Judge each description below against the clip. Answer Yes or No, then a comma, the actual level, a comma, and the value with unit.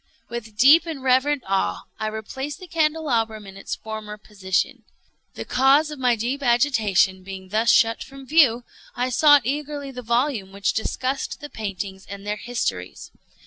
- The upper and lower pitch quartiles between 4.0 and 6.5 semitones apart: Yes, average, 4.9 semitones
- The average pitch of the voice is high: Yes, high, 235 Hz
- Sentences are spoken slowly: No, average, 160 wpm